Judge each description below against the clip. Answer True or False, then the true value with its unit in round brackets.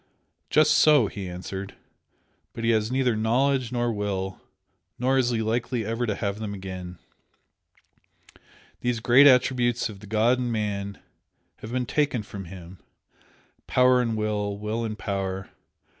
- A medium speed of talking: True (145 wpm)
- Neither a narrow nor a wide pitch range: True (3.5 semitones)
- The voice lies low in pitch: True (110 Hz)